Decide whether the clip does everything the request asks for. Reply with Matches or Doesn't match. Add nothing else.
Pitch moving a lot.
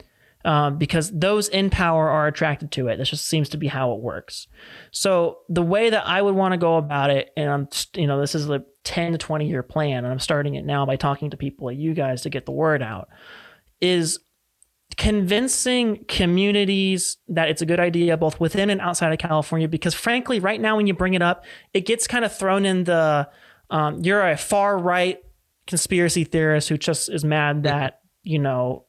Doesn't match